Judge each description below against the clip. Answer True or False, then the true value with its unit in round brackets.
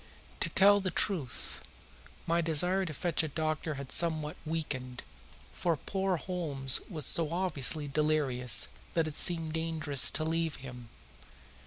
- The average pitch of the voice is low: False (160 Hz)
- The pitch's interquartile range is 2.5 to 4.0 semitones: True (3.0 semitones)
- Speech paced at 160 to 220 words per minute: False (140 wpm)